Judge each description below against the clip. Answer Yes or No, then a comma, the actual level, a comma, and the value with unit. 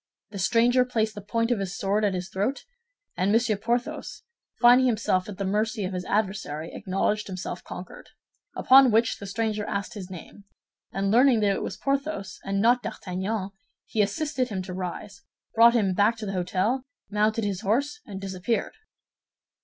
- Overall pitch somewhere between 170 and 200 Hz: No, high, 210 Hz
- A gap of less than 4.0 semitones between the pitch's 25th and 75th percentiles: Yes, average, 3.2 semitones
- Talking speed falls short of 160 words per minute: No, average, 175 wpm